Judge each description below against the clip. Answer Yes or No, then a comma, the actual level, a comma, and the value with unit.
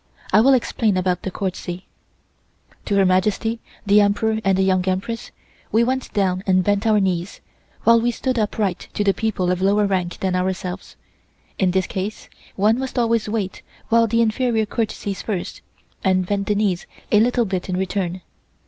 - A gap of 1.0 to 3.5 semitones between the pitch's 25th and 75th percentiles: Yes, average, 3.0 semitones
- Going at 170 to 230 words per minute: Yes, average, 175 wpm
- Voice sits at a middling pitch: No, high, 200 Hz